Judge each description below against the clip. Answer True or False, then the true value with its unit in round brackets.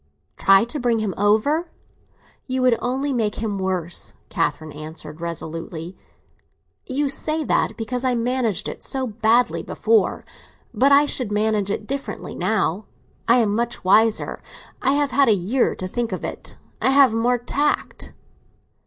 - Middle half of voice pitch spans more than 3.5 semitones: True (4.9 semitones)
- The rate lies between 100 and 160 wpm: True (155 wpm)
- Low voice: False (230 Hz)